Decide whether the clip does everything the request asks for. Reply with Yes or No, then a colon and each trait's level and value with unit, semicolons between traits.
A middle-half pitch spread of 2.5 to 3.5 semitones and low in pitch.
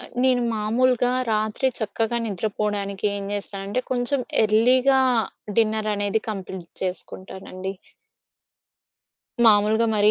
No: average, 2.9 semitones; high, 215 Hz